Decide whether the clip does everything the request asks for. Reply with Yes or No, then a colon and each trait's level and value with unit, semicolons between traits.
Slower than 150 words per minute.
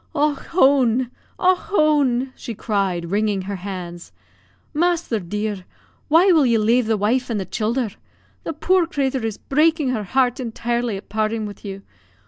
No: average, 155 wpm